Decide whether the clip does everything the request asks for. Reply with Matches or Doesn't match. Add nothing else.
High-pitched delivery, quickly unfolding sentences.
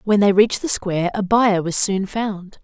Matches